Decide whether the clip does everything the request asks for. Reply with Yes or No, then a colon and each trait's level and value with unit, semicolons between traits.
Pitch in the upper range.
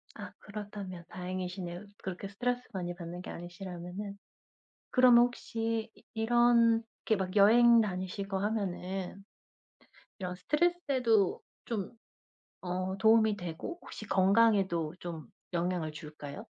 Yes: high, 195 Hz